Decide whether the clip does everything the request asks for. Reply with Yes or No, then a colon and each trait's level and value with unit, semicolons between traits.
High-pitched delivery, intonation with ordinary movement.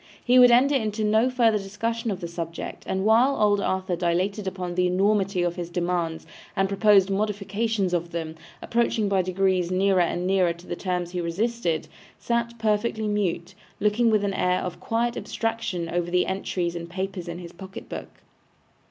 Yes: high, 195 Hz; average, 3.4 semitones